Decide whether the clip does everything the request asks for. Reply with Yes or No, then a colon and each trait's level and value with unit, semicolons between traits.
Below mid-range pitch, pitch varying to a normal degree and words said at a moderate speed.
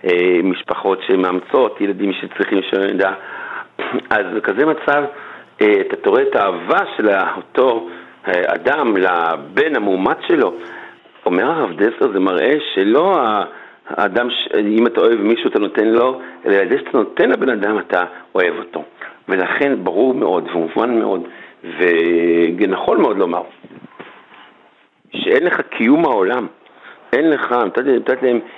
No: low, 105 Hz; wide, 6.4 semitones; average, 130 wpm